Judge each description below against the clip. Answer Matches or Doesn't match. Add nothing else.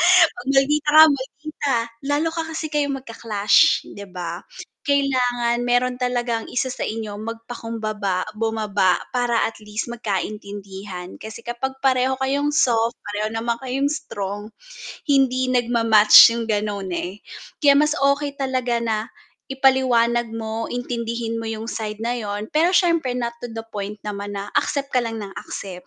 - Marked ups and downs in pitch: Doesn't match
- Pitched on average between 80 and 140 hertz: Doesn't match